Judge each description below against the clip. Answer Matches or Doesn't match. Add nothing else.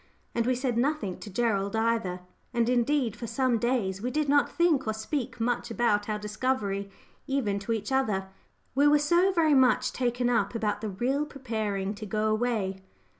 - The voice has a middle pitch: Doesn't match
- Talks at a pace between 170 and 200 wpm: Matches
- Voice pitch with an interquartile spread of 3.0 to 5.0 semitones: Matches